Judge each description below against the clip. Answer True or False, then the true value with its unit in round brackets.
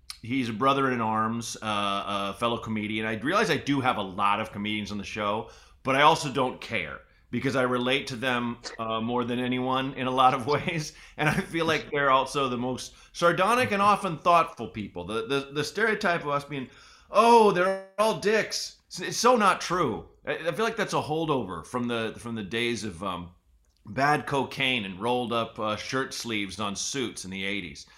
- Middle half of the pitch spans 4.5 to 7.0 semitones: True (5.3 semitones)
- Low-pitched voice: True (125 Hz)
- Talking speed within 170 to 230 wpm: True (205 wpm)